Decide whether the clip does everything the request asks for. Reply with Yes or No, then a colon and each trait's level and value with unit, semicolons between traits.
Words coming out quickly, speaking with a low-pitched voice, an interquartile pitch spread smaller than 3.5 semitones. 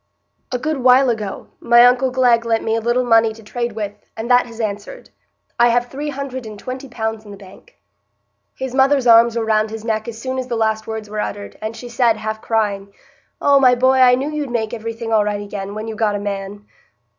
No: fast, 225 wpm; high, 230 Hz; narrow, 2.5 semitones